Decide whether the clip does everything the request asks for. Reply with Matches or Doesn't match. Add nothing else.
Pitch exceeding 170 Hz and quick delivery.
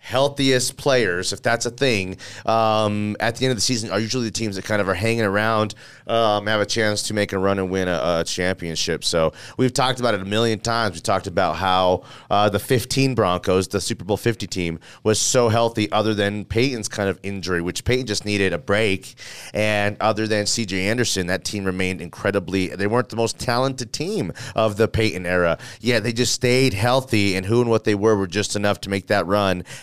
Doesn't match